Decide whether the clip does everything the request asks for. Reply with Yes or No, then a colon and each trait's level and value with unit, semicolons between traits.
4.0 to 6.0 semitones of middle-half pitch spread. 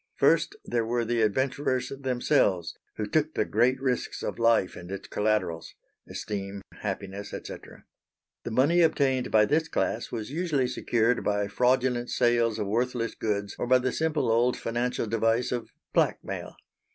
No: average, 3.4 semitones